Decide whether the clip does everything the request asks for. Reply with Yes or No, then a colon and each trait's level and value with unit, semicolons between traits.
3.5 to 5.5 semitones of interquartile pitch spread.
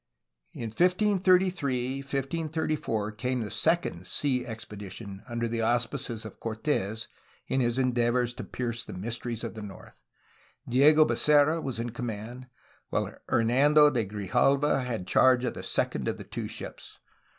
Yes: average, 4.1 semitones